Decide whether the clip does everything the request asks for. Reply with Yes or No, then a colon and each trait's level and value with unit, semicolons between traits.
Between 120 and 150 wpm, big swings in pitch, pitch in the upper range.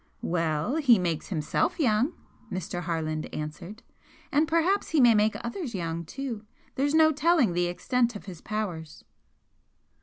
Yes: average, 145 wpm; wide, 8.6 semitones; high, 215 Hz